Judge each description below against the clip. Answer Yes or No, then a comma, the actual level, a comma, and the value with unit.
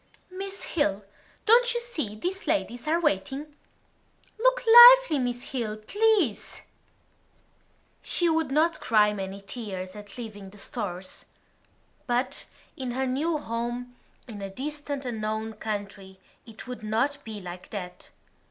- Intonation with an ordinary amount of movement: No, wide, 6.9 semitones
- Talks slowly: Yes, slow, 130 wpm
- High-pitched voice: Yes, high, 245 Hz